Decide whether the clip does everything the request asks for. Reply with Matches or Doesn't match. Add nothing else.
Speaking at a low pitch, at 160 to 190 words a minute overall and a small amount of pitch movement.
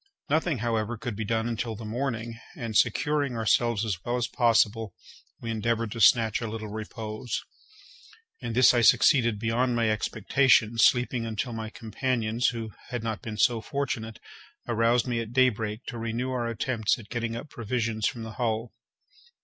Matches